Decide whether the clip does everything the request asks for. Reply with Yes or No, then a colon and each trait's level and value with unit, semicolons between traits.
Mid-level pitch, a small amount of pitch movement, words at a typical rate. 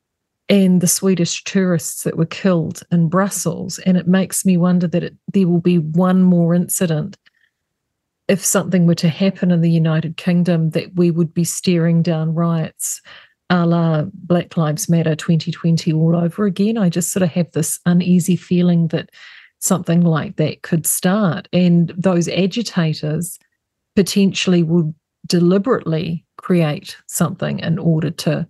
Yes: medium, 175 Hz; narrow, 1.8 semitones; average, 150 wpm